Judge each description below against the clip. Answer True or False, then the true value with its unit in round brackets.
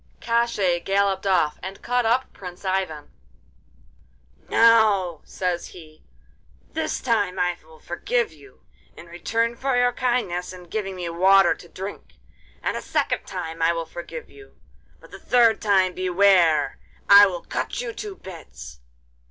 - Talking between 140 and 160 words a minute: True (145 wpm)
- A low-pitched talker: False (190 Hz)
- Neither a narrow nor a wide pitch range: True (4.9 semitones)